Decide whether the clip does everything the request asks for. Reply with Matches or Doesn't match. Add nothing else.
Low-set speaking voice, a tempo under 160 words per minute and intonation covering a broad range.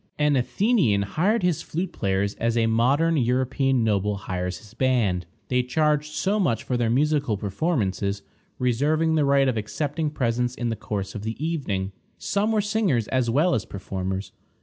Doesn't match